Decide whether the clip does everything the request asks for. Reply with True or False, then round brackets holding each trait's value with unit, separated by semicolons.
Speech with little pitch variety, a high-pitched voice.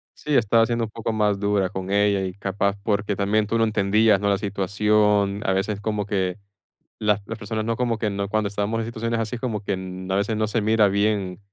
False (1.7 semitones; 105 Hz)